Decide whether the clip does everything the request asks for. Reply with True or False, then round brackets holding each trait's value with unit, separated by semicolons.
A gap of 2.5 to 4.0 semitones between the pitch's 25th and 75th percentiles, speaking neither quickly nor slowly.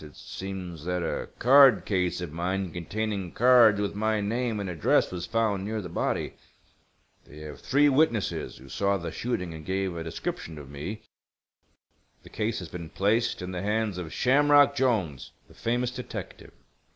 False (4.6 semitones; 170 wpm)